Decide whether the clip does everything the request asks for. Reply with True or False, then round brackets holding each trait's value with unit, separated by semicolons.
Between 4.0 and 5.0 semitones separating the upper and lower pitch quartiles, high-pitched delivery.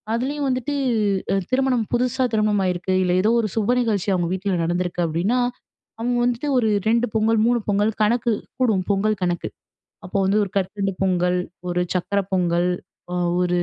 True (4.6 semitones; 205 Hz)